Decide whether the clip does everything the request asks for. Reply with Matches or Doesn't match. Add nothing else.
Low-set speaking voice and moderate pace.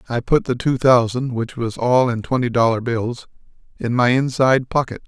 Matches